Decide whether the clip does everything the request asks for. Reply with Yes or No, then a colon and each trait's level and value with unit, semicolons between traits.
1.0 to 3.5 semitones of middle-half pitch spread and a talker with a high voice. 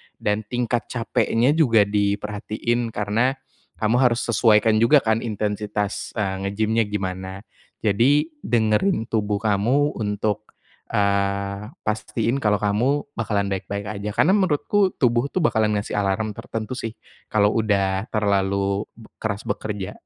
No: narrow, 2.4 semitones; low, 105 Hz